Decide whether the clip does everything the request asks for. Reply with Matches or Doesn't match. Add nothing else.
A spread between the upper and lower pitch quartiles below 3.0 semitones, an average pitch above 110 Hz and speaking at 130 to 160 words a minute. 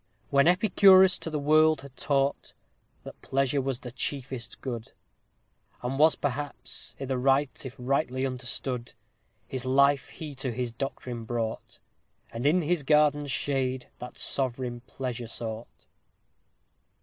Matches